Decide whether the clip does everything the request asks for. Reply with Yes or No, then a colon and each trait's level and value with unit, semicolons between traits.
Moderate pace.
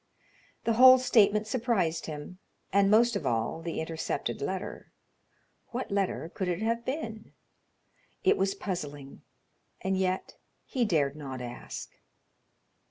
No: slow, 125 wpm